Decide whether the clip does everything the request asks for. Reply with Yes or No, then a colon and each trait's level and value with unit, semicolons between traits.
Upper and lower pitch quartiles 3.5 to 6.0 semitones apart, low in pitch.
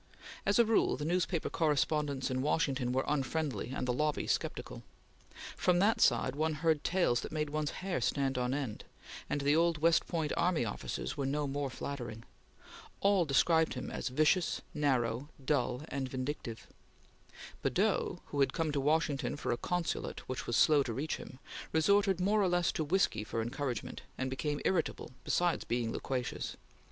No: average, 4.0 semitones; medium, 145 Hz